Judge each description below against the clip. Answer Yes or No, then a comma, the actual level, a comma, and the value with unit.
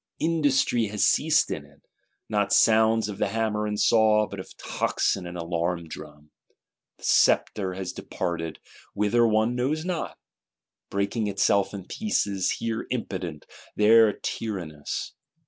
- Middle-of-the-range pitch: No, low, 105 Hz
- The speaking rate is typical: No, slow, 130 wpm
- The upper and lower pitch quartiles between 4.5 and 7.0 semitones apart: No, average, 3.4 semitones